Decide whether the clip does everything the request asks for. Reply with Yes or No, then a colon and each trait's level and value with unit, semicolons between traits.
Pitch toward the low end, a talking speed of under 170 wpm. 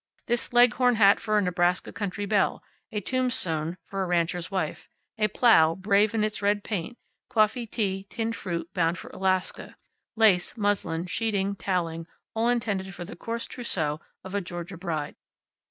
No: high, 195 Hz; average, 160 wpm